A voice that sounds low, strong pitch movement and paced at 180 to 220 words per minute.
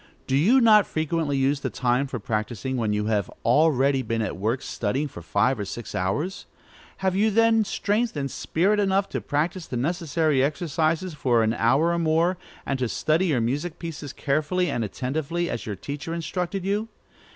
No: medium, 150 Hz; wide, 5.8 semitones; average, 185 wpm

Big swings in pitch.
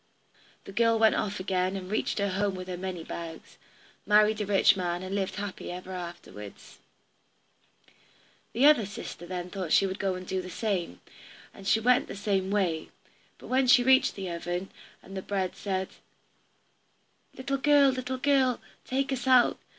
No: average, 4.3 semitones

